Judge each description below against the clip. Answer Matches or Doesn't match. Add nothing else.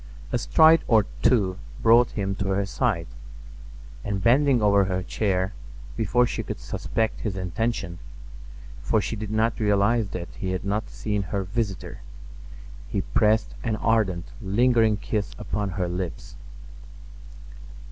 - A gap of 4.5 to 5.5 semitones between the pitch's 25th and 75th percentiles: Doesn't match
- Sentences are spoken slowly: Matches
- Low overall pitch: Matches